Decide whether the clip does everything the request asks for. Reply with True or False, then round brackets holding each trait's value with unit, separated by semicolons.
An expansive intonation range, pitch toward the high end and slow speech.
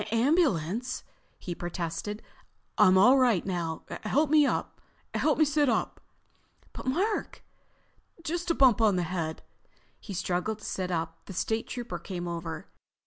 True (6.9 semitones; 205 Hz; 130 wpm)